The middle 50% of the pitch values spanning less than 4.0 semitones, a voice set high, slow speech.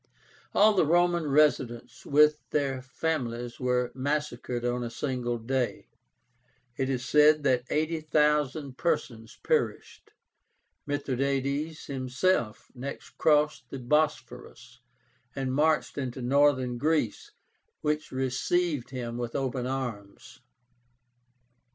No: average, 3.4 semitones; low, 135 Hz; slow, 100 wpm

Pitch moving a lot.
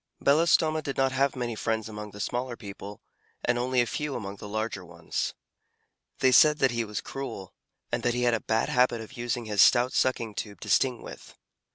No: average, 3.3 semitones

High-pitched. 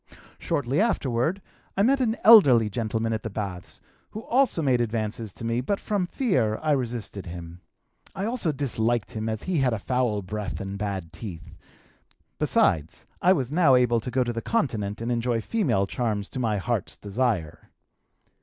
No: low, 120 Hz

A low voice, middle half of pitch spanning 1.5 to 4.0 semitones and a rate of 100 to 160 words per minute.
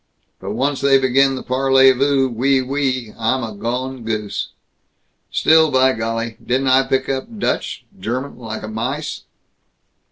Yes: low, 130 Hz; average, 2.7 semitones; average, 150 wpm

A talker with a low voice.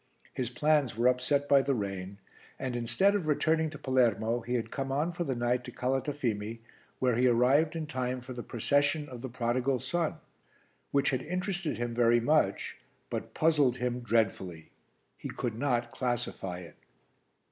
Yes: low, 125 Hz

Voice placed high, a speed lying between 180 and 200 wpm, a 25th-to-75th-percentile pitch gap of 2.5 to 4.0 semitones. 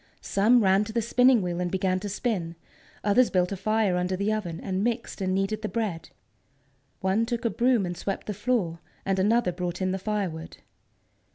Yes: high, 195 Hz; average, 195 wpm; average, 3.3 semitones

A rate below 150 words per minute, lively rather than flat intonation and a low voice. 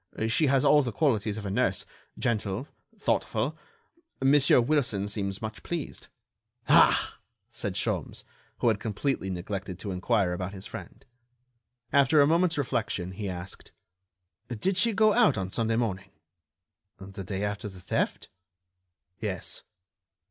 Yes: slow, 135 wpm; wide, 5.9 semitones; low, 110 Hz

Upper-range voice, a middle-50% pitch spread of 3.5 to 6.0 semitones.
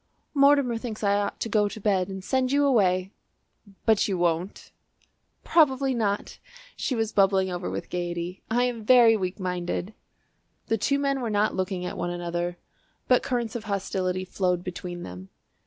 Yes: high, 200 Hz; average, 4.7 semitones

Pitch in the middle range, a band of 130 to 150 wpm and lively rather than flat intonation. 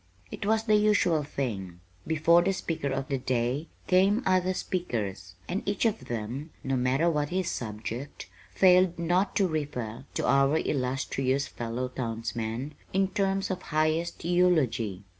Yes: medium, 150 Hz; average, 145 wpm; wide, 6.5 semitones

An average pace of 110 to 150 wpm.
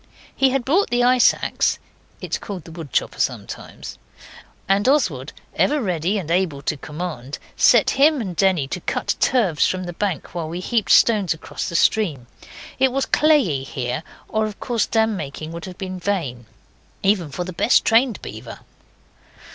No: average, 175 wpm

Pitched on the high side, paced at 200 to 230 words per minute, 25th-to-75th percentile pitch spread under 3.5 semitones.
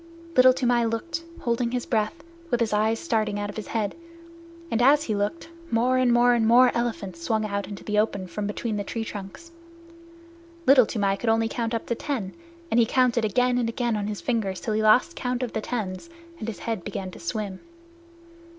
Yes: high, 225 Hz; fast, 205 wpm; average, 2.8 semitones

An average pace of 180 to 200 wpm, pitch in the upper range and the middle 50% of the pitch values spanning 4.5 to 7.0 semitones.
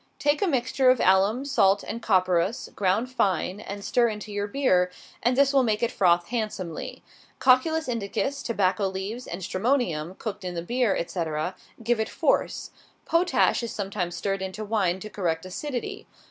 No: average, 165 wpm; high, 205 Hz; average, 4.8 semitones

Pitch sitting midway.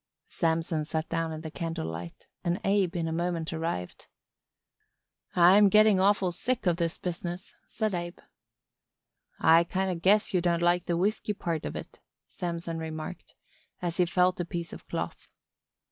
Yes: medium, 175 Hz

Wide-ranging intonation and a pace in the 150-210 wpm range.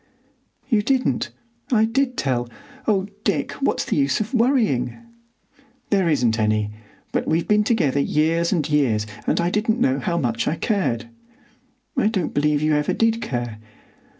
Yes: wide, 8.5 semitones; average, 155 wpm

